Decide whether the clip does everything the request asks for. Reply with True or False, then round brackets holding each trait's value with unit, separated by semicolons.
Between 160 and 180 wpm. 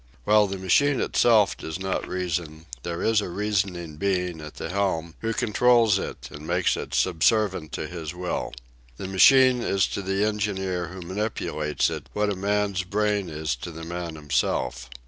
True (170 wpm)